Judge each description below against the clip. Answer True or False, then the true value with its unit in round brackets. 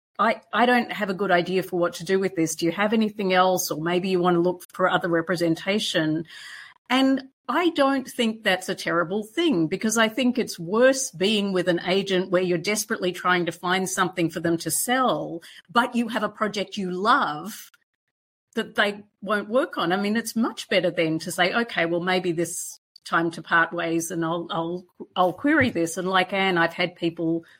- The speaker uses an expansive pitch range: False (4.1 semitones)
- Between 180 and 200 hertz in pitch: True (185 Hz)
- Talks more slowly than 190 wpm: False (205 wpm)